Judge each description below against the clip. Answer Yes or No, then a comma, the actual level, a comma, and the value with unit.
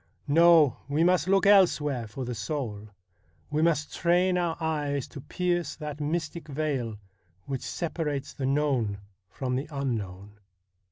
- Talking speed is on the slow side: No, average, 145 wpm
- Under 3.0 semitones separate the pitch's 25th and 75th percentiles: No, average, 4.5 semitones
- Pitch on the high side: No, medium, 150 Hz